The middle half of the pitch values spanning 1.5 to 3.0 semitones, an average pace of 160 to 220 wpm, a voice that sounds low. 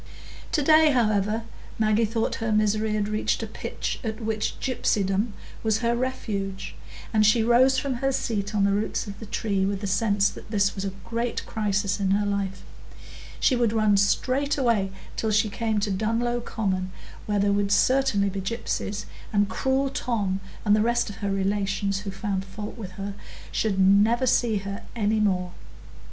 No: narrow, 2.6 semitones; average, 180 wpm; high, 210 Hz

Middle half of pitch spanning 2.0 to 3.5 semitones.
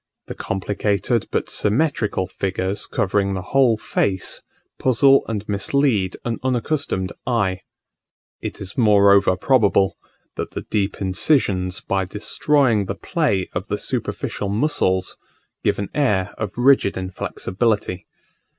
No: average, 4.5 semitones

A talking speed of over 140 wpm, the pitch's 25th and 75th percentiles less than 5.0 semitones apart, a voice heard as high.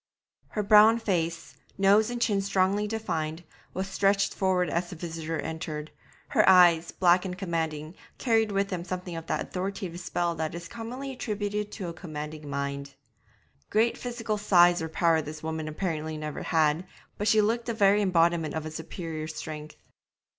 No: average, 170 wpm; average, 4.3 semitones; medium, 175 Hz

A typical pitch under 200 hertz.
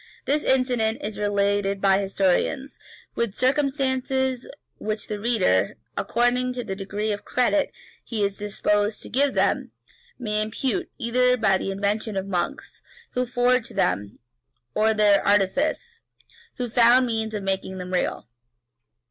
No: high, 220 Hz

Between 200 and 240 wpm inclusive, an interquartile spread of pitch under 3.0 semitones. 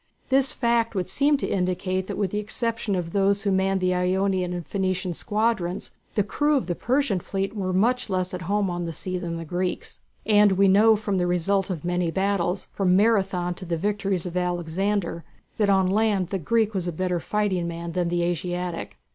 Yes: fast, 205 wpm; narrow, 2.6 semitones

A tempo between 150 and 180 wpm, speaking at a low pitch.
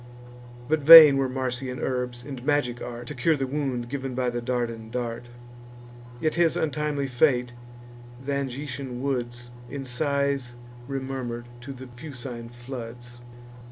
No: slow, 135 wpm; low, 130 Hz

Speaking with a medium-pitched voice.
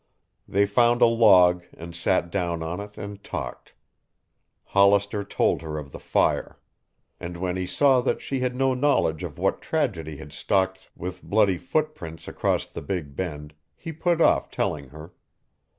No: very low, 95 Hz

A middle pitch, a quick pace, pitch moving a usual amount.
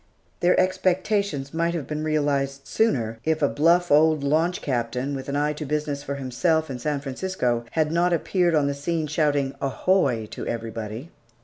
No: medium, 150 Hz; average, 175 wpm; average, 3.4 semitones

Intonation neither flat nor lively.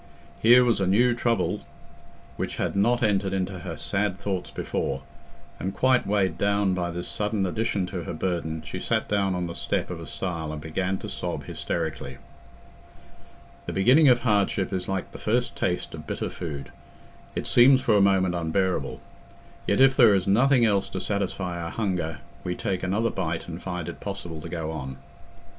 Yes: average, 3.3 semitones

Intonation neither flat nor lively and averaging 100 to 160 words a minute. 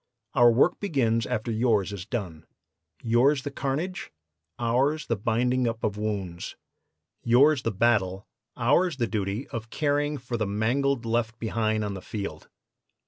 Yes: average, 3.8 semitones; average, 145 wpm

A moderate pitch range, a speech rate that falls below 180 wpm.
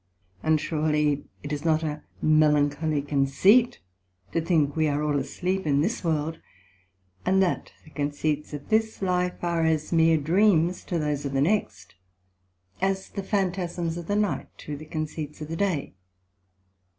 Yes: average, 3.3 semitones; average, 160 wpm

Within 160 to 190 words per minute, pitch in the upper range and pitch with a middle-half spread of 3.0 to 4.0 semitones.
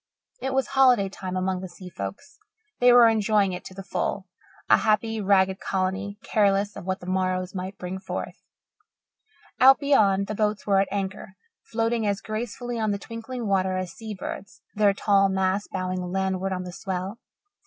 No: average, 175 wpm; high, 195 Hz; narrow, 2.5 semitones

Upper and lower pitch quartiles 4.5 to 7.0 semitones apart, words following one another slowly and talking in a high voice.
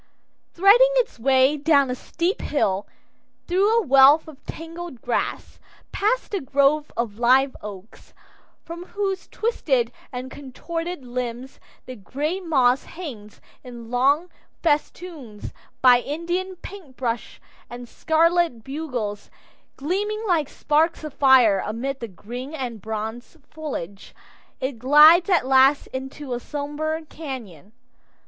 Yes: average, 5.2 semitones; slow, 120 wpm; very high, 275 Hz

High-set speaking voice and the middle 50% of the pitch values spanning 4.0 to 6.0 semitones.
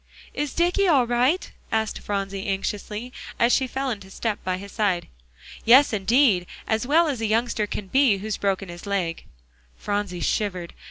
Yes: high, 215 Hz; average, 4.3 semitones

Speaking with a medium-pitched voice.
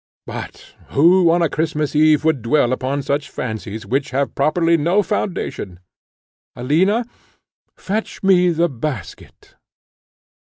Yes: medium, 155 Hz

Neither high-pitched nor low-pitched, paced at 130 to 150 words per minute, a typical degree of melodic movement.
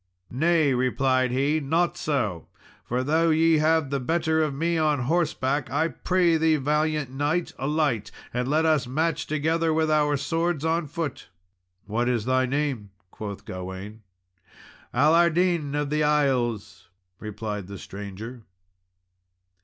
Yes: medium, 145 Hz; slow, 135 wpm; average, 4.3 semitones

